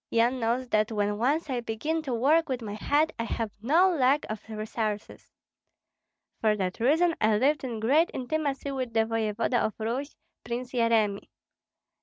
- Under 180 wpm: Yes, average, 165 wpm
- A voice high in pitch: Yes, high, 240 Hz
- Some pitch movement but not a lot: Yes, average, 4.3 semitones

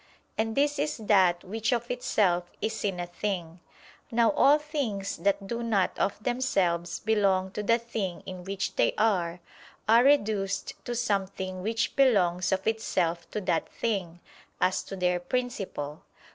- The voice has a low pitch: No, high, 200 Hz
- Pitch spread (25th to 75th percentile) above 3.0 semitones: Yes, average, 4.1 semitones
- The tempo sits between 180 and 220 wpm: No, average, 155 wpm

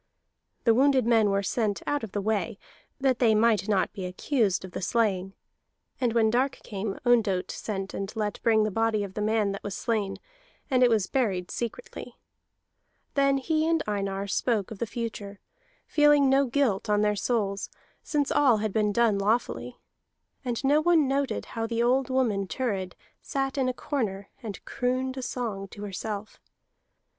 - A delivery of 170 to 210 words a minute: Yes, average, 175 wpm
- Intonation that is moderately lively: Yes, average, 4.2 semitones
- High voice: Yes, high, 225 Hz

